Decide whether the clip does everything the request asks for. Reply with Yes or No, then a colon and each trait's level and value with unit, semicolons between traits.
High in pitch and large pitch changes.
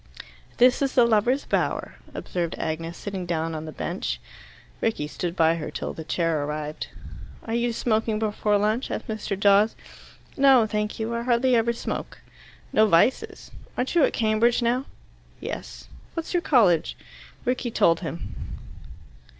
Yes: high, 215 Hz; wide, 5.9 semitones